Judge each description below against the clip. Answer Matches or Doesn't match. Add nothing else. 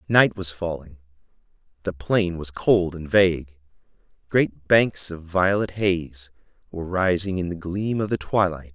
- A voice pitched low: Matches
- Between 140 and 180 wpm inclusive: Matches